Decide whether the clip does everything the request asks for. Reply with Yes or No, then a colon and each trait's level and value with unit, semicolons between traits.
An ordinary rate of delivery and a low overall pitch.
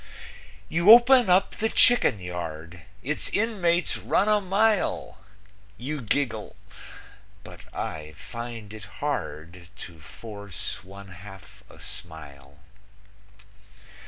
No: slow, 100 wpm; low, 105 Hz